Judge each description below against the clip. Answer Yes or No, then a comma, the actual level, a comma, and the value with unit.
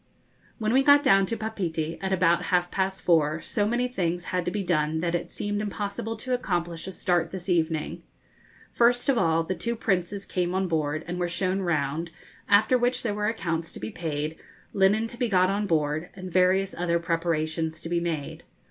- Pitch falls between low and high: Yes, medium, 180 Hz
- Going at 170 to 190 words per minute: No, average, 200 wpm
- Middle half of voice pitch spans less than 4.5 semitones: Yes, average, 3.7 semitones